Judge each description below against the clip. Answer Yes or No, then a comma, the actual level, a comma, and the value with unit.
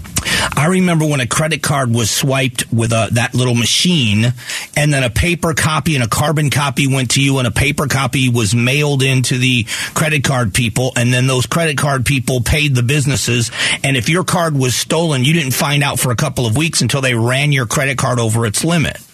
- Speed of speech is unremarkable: No, fast, 215 wpm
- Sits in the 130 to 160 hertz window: Yes, low, 135 Hz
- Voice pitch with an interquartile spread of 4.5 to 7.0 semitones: No, average, 3.4 semitones